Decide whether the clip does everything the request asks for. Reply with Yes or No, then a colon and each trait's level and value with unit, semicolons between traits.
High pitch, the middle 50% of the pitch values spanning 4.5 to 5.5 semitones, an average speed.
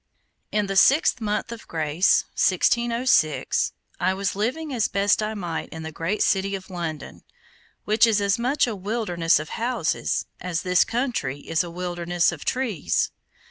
Yes: high, 195 Hz; average, 5.1 semitones; average, 160 wpm